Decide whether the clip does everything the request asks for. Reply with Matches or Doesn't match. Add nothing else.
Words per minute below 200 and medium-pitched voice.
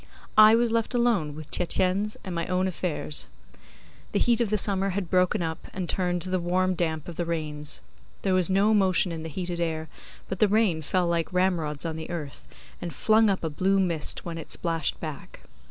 Doesn't match